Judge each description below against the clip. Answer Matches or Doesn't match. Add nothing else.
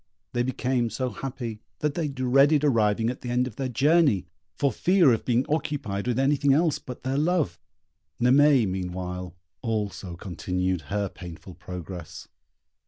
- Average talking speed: Matches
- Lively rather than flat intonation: Matches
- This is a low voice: Matches